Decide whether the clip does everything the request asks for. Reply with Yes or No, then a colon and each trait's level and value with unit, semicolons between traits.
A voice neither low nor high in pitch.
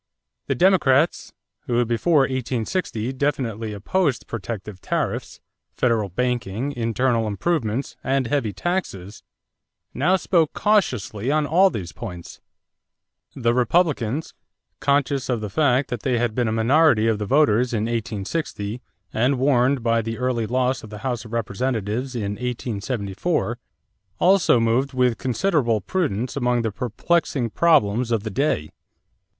No: low, 125 Hz